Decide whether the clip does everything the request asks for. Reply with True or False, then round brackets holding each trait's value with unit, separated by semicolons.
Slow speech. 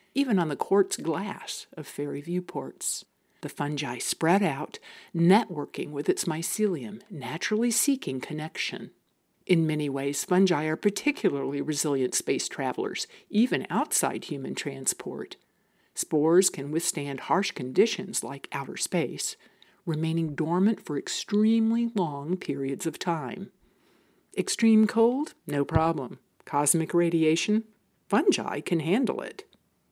True (115 wpm)